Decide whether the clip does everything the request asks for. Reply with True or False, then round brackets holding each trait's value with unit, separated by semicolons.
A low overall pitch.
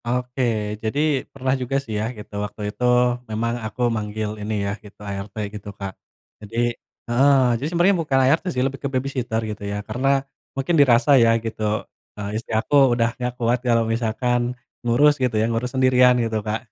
True (120 Hz)